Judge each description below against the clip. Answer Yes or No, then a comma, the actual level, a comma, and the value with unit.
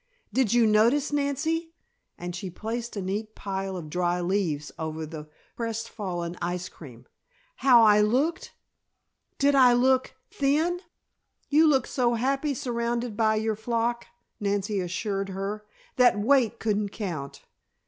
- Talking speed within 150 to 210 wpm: No, average, 140 wpm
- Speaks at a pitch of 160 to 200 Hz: No, high, 220 Hz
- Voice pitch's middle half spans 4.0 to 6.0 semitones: Yes, average, 4.9 semitones